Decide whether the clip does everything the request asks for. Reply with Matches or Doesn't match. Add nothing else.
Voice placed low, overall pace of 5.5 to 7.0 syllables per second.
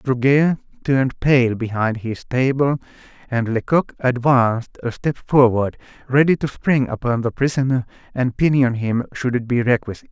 Doesn't match